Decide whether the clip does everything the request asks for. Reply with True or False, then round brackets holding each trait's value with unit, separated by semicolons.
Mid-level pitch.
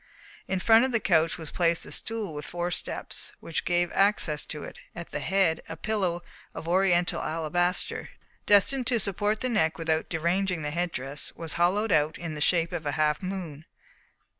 True (175 Hz)